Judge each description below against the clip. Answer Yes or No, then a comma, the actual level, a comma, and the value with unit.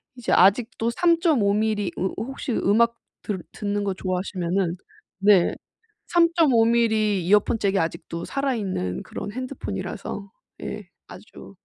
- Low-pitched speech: No, high, 210 Hz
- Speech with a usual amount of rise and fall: Yes, average, 3.6 semitones